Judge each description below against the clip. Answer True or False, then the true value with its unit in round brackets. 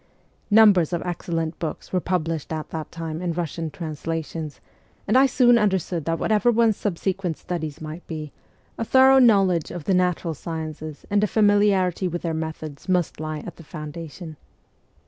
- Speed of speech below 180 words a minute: True (165 wpm)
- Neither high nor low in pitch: True (170 Hz)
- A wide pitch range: False (3.6 semitones)